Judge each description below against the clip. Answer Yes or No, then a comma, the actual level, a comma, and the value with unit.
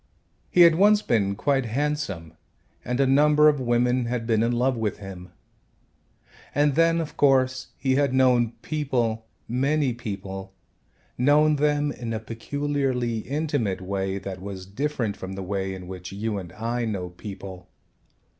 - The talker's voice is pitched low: Yes, low, 120 Hz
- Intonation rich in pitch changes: Yes, wide, 6.4 semitones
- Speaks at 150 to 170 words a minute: Yes, average, 155 wpm